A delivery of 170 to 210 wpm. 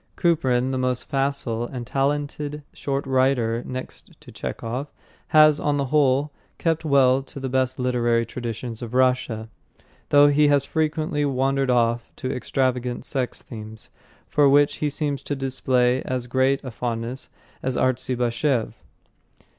No: average, 145 wpm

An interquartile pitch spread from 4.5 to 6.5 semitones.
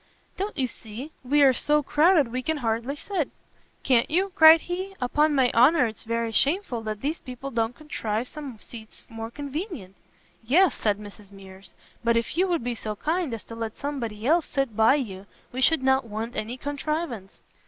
Yes: average, 5.1 semitones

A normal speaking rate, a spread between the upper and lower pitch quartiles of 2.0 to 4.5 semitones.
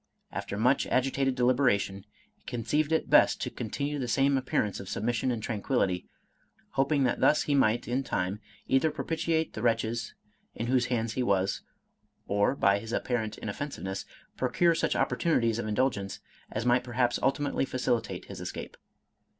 Yes: average, 160 wpm; average, 3.8 semitones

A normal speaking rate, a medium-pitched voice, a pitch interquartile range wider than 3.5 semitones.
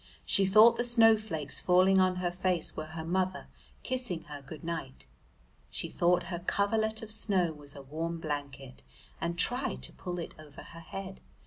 Yes: average, 175 wpm; medium, 180 Hz; average, 4.2 semitones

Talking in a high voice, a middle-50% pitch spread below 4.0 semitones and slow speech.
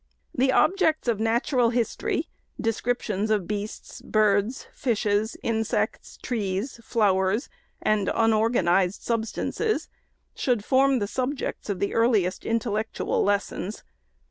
Yes: high, 220 Hz; average, 3.1 semitones; slow, 115 wpm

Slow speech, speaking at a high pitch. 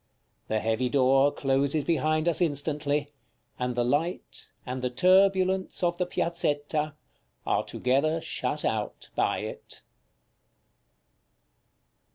No: slow, 110 wpm; medium, 145 Hz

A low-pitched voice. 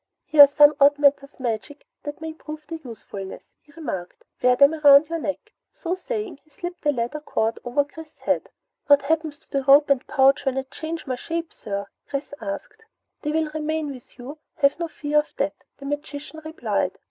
No: very high, 290 Hz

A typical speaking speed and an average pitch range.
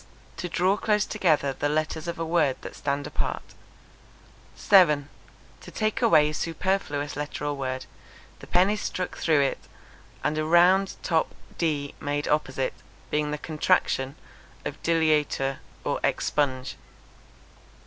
No: slow, 130 wpm; average, 3.2 semitones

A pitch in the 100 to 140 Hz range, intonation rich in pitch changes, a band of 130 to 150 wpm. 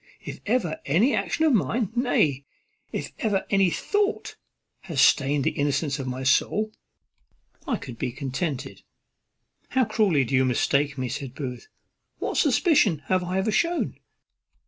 No: medium, 160 Hz; wide, 8.2 semitones; average, 145 wpm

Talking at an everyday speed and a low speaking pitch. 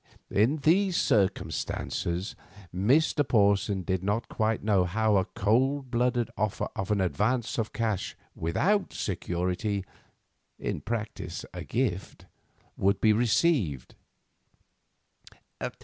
No: slow, 100 wpm; low, 105 Hz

